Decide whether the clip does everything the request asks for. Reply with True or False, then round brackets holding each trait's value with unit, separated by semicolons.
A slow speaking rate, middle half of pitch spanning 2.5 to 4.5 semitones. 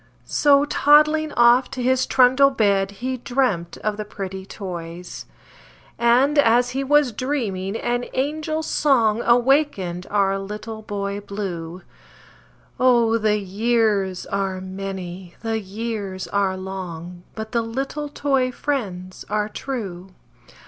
False (120 wpm; 5.0 semitones)